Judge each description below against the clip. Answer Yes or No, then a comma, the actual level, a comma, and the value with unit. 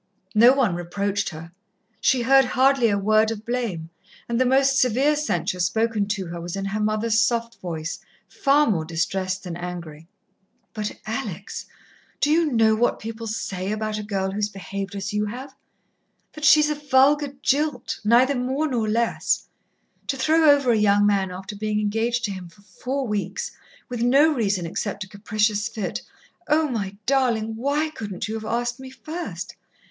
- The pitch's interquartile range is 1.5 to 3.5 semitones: No, average, 4.7 semitones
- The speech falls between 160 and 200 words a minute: Yes, average, 175 wpm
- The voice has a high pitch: Yes, high, 220 Hz